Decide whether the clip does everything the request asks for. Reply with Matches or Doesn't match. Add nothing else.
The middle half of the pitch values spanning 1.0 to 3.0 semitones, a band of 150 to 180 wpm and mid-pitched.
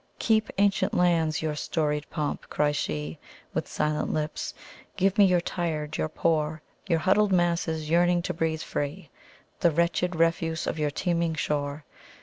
Doesn't match